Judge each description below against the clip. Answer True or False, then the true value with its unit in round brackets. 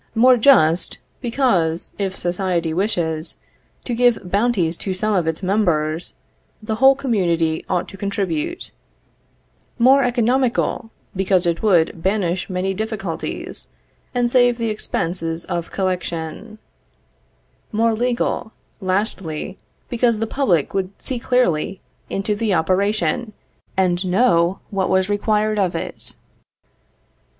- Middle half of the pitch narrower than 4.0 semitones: False (4.7 semitones)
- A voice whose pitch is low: False (195 Hz)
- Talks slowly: True (115 wpm)